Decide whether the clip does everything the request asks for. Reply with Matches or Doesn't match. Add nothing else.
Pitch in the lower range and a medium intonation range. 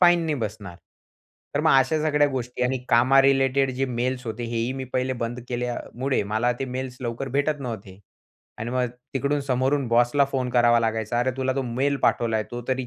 Doesn't match